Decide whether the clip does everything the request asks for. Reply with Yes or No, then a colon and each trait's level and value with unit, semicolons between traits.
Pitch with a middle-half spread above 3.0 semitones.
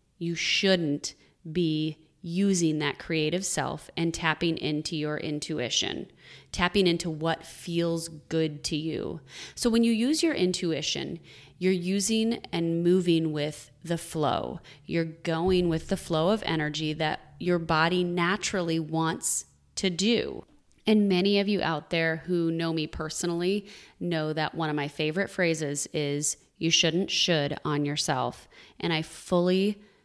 No: average, 2.7 semitones